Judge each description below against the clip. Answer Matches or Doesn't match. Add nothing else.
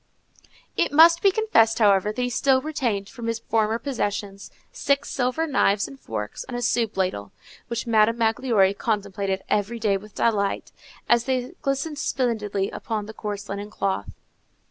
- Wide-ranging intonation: Doesn't match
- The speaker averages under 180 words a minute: Matches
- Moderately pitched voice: Doesn't match